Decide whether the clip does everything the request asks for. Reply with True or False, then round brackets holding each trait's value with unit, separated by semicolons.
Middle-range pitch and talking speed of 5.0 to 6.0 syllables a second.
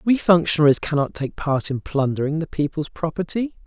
True (160 Hz; 5.5 syllables/s)